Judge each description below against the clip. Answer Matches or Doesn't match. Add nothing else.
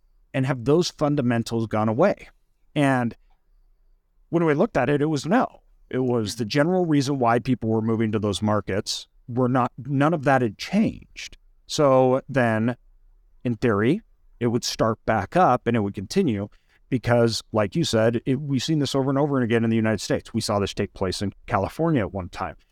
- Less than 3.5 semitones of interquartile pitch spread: Doesn't match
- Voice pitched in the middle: Doesn't match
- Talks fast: Doesn't match